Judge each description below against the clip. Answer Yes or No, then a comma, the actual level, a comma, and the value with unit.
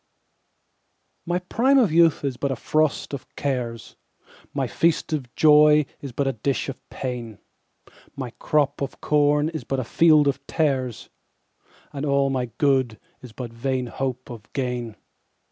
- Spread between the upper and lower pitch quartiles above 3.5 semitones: No, average, 3.2 semitones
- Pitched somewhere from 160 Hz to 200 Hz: No, low, 135 Hz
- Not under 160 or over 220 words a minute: No, average, 145 wpm